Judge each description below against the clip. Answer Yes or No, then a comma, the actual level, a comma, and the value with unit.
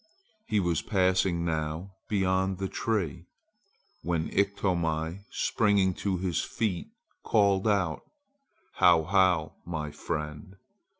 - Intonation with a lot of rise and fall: No, average, 3.2 semitones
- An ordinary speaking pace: No, slow, 105 wpm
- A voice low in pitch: Yes, very low, 90 Hz